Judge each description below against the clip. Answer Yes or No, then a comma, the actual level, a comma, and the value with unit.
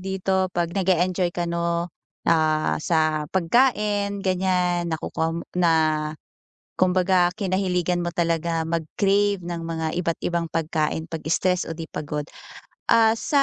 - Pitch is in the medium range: Yes, medium, 175 Hz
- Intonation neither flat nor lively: No, narrow, 2.3 semitones